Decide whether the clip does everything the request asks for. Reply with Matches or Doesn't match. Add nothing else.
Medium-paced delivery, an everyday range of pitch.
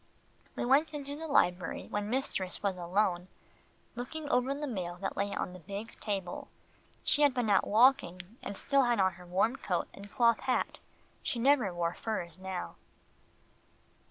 Doesn't match